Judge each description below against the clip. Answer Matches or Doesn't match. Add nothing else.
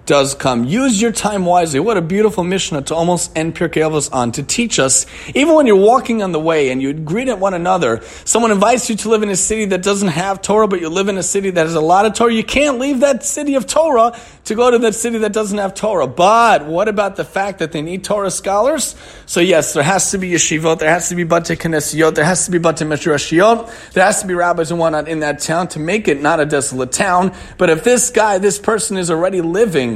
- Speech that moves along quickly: Matches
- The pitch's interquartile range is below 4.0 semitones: Doesn't match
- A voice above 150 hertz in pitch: Matches